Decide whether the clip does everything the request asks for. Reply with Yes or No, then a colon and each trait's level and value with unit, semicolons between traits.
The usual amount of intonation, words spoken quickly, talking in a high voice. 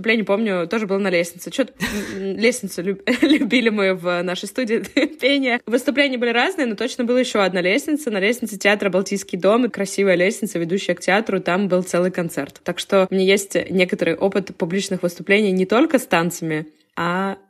Yes: average, 4.1 semitones; fast, 180 wpm; high, 195 Hz